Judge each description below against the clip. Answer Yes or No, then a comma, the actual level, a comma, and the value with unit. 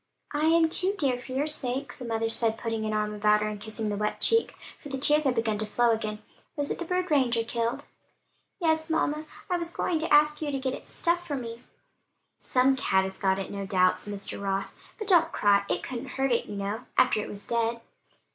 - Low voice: No, high, 245 Hz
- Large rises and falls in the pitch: Yes, wide, 6.0 semitones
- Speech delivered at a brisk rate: Yes, fast, 230 wpm